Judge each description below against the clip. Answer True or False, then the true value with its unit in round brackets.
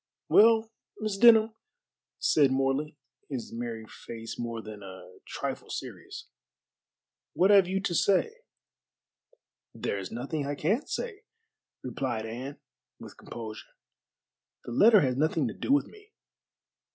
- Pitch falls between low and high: True (145 Hz)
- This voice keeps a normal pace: False (125 wpm)